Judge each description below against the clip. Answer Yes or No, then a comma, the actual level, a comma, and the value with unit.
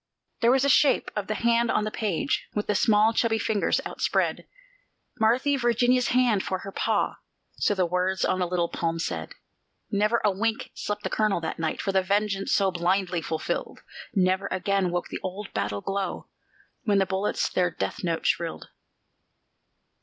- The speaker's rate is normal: Yes, average, 175 wpm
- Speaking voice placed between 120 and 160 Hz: No, high, 200 Hz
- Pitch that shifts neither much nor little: Yes, average, 3.2 semitones